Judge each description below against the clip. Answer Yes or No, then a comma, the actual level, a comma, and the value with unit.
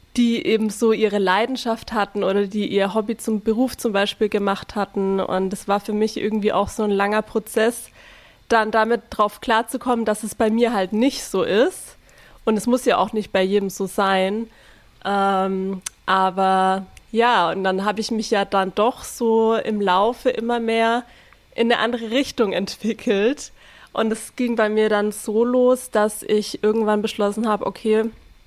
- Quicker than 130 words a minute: Yes, average, 175 wpm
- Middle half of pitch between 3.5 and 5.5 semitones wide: No, narrow, 2.4 semitones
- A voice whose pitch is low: No, high, 215 Hz